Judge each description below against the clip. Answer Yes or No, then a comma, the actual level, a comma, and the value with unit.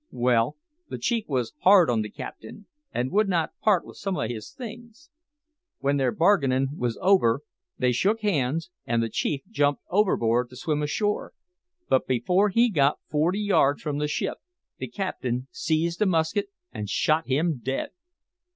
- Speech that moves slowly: No, average, 165 wpm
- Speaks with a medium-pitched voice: Yes, medium, 150 Hz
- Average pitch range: No, wide, 7.5 semitones